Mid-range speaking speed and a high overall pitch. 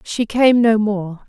Yes: average, 190 wpm; high, 215 Hz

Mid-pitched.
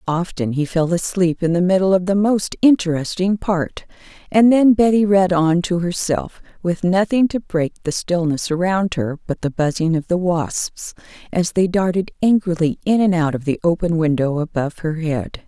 Yes: medium, 175 Hz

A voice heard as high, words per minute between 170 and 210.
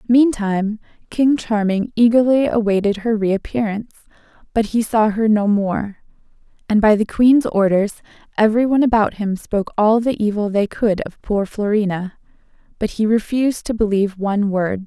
No: high, 215 Hz; average, 155 wpm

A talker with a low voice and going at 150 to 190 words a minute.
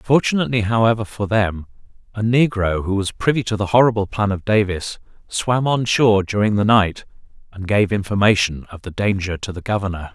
Yes: low, 105 Hz; average, 175 wpm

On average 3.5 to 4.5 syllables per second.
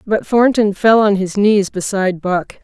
Yes: 4.4 syllables/s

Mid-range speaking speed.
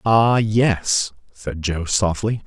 No: slow, 120 wpm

